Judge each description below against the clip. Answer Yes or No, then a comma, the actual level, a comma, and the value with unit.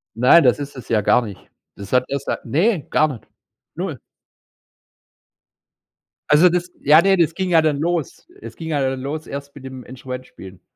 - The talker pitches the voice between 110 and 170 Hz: Yes, medium, 140 Hz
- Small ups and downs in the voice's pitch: No, average, 4.4 semitones